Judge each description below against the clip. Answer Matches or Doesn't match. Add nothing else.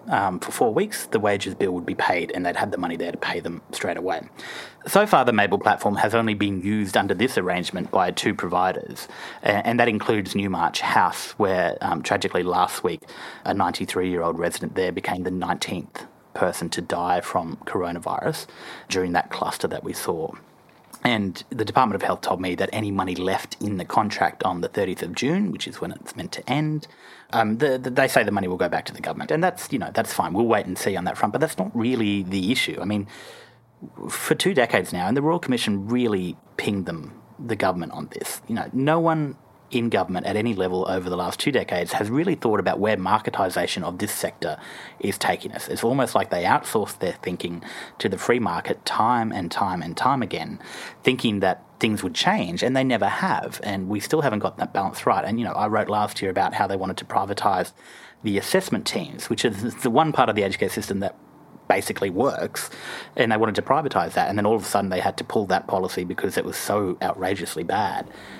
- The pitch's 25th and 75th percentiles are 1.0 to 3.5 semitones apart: Doesn't match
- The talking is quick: Matches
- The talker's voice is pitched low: Matches